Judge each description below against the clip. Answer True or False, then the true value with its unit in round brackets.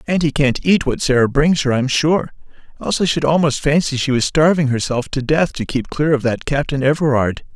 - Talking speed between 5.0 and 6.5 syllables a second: True (5.5 syllables/s)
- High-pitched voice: False (145 Hz)